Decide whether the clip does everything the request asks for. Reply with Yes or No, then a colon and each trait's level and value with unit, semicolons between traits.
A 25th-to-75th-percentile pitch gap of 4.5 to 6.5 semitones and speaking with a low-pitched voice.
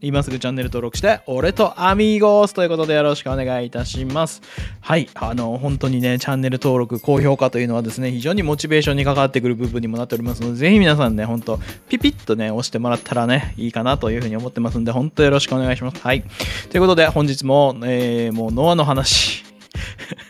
No: average, 3.6 semitones; low, 125 Hz